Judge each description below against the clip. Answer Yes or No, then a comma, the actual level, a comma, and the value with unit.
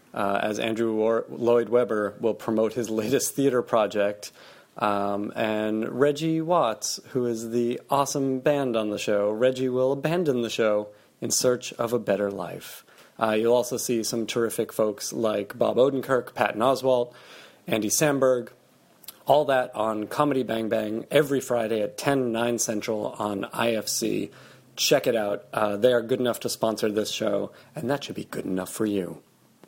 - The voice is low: Yes, low, 115 Hz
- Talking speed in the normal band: Yes, average, 170 wpm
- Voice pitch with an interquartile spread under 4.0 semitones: Yes, average, 3.0 semitones